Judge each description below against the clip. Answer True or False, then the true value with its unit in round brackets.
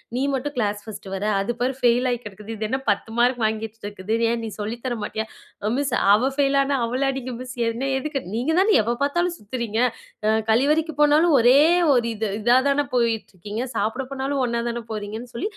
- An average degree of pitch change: True (3.7 semitones)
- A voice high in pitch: True (240 Hz)